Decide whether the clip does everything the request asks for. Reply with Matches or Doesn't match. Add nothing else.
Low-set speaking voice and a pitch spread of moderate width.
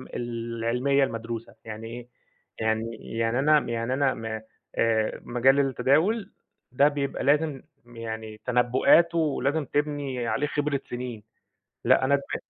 Matches